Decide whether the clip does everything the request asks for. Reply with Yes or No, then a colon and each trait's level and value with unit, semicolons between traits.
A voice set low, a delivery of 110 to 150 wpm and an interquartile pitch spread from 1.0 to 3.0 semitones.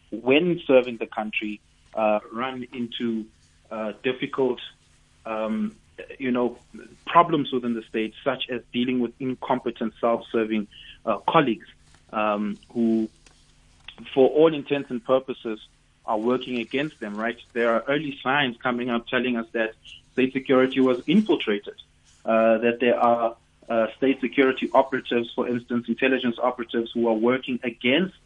Yes: low, 120 Hz; average, 140 wpm; narrow, 2.5 semitones